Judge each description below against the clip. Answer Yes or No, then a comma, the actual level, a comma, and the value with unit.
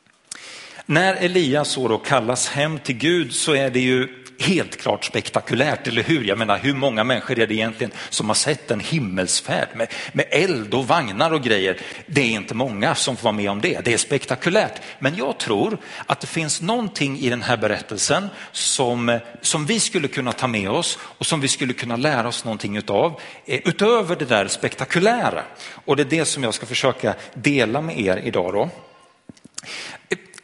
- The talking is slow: No, average, 185 wpm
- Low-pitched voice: Yes, low, 130 Hz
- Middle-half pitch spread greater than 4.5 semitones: Yes, average, 5.0 semitones